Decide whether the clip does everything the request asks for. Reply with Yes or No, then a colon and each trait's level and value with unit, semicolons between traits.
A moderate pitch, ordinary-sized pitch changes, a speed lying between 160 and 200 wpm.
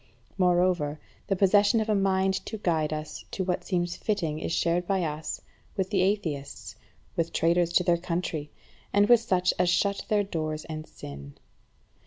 Yes: medium, 180 Hz; average, 3.6 semitones; average, 165 wpm